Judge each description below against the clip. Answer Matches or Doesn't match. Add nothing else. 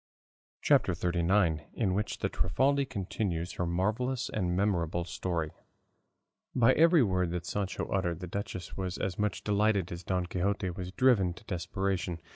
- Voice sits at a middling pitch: Doesn't match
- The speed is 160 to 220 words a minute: Doesn't match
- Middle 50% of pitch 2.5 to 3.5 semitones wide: Matches